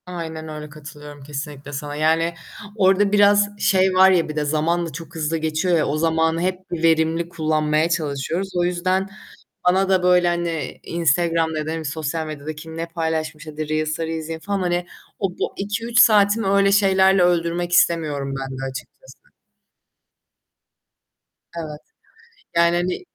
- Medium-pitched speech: Yes, medium, 165 Hz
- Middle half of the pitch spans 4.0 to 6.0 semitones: No, average, 2.9 semitones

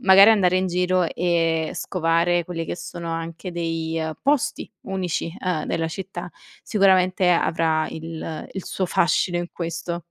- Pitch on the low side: No, medium, 175 Hz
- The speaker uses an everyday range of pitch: No, narrow, 2.0 semitones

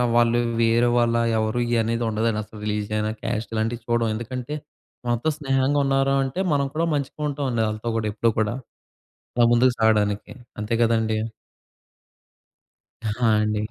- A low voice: Yes, low, 115 Hz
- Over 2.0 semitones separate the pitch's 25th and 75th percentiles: Yes, average, 2.8 semitones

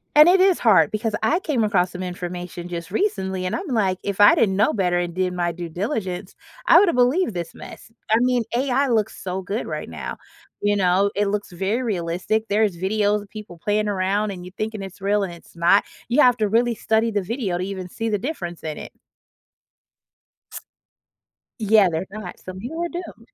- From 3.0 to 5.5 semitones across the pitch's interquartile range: Yes, average, 3.7 semitones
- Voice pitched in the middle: No, high, 205 Hz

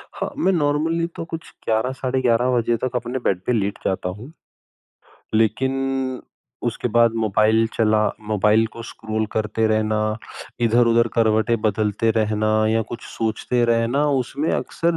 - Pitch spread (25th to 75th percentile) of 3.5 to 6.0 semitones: No, average, 2.8 semitones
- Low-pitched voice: Yes, low, 115 Hz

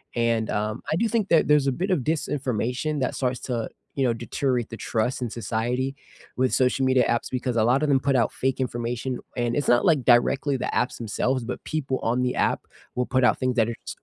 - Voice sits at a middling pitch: No, low, 125 Hz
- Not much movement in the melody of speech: Yes, narrow, 2.3 semitones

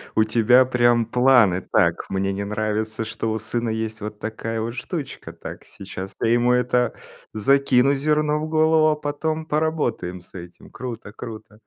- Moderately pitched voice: No, low, 120 Hz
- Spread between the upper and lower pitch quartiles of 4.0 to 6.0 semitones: Yes, average, 4.3 semitones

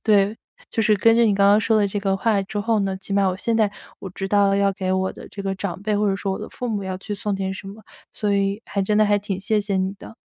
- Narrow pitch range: Yes, narrow, 1.5 semitones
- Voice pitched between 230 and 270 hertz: No, high, 200 Hz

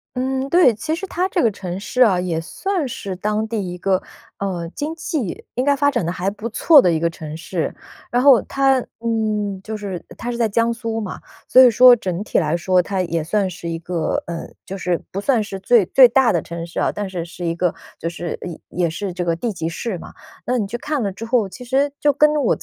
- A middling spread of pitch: No, wide, 5.9 semitones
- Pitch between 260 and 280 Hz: No, high, 205 Hz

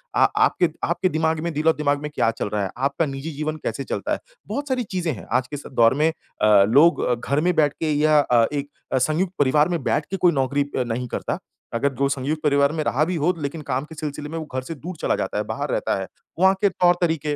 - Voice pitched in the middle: Yes, medium, 150 Hz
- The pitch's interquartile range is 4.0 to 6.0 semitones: No, average, 3.3 semitones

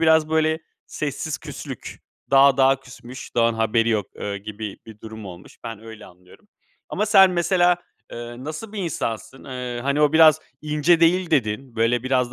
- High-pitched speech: No, low, 130 Hz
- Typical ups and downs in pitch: No, wide, 5.9 semitones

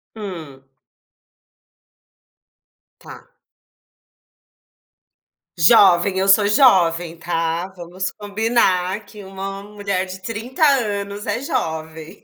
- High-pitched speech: Yes, high, 195 Hz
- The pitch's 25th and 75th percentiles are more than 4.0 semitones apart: No, average, 3.2 semitones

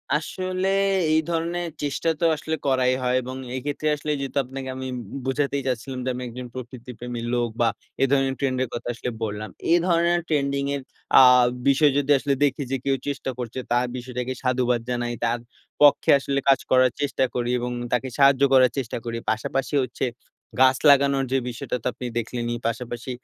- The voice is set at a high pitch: No, low, 130 Hz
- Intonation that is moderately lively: No, narrow, 2.2 semitones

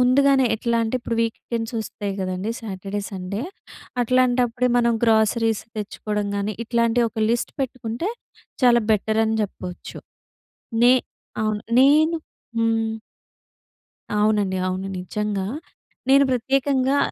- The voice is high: Yes, high, 225 Hz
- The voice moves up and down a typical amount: Yes, average, 3.0 semitones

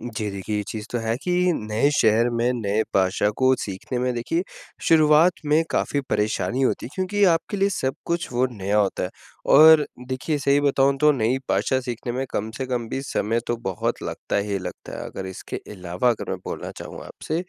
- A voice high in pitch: No, low, 125 Hz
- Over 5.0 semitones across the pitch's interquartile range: Yes, wide, 5.4 semitones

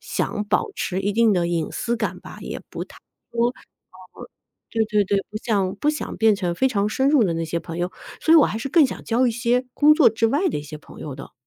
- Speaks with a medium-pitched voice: No, high, 220 Hz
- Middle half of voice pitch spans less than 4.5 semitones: No, average, 5.2 semitones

